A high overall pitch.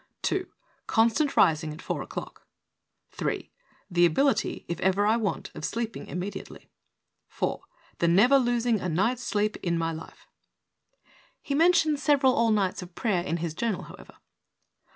Yes: high, 210 Hz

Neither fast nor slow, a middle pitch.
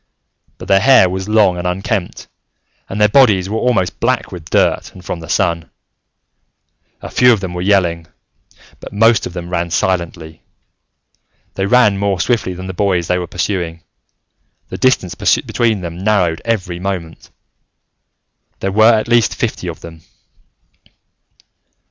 No: average, 150 wpm; very low, 95 Hz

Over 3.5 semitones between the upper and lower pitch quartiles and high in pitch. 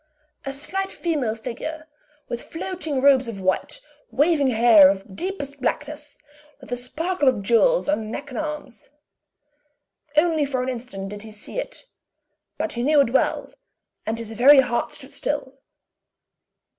Yes: average, 4.7 semitones; very high, 265 Hz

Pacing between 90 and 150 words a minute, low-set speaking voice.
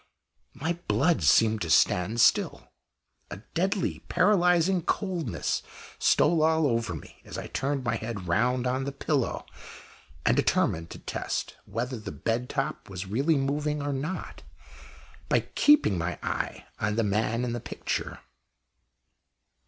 Yes: average, 140 wpm; low, 130 Hz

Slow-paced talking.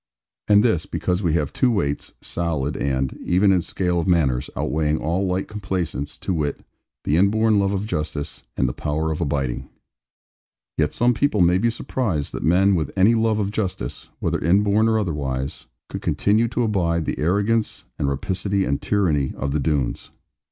No: average, 175 wpm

